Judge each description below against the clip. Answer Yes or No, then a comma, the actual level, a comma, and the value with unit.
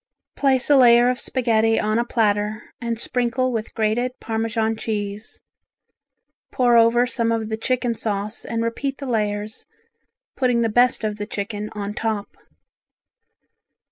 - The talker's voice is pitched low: No, high, 230 Hz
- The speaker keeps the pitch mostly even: Yes, narrow, 2.2 semitones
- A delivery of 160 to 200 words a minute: No, average, 140 wpm